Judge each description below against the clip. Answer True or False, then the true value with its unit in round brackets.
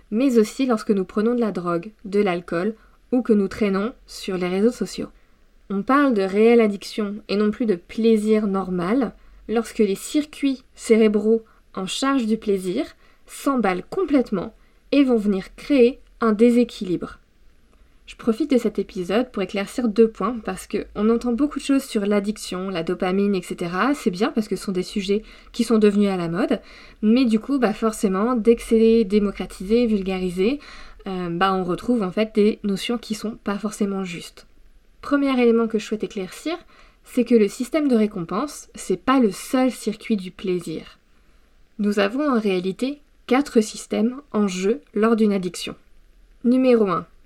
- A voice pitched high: True (215 Hz)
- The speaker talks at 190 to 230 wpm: False (170 wpm)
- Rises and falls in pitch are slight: False (3.5 semitones)